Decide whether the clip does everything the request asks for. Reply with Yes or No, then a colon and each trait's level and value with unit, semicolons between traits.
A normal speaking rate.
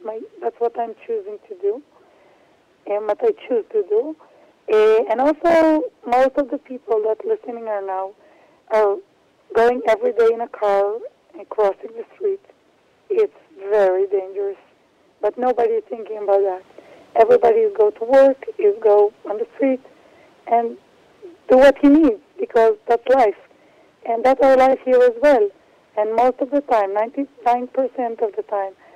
Yes: average, 165 wpm